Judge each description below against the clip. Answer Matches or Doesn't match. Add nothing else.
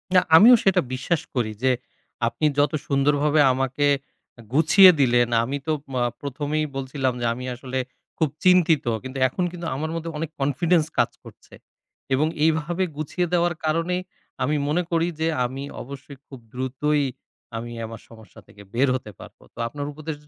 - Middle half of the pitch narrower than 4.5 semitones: Matches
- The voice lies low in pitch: Doesn't match